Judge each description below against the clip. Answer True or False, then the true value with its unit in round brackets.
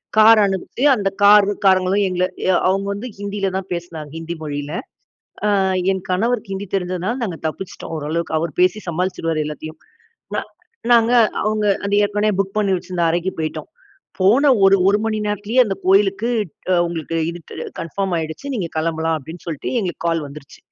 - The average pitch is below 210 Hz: True (185 Hz)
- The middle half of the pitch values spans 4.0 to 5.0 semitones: False (3.6 semitones)